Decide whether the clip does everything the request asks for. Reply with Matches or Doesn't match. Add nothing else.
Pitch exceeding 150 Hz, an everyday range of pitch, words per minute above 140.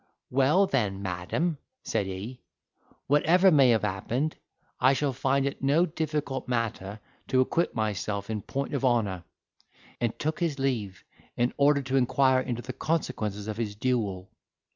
Doesn't match